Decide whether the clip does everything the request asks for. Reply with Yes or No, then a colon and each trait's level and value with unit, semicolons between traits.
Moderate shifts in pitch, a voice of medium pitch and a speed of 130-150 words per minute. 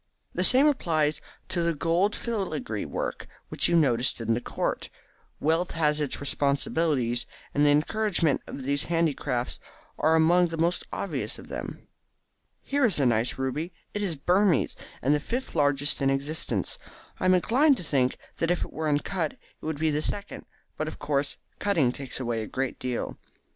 No: average, 4.2 semitones; medium, 155 Hz; average, 175 wpm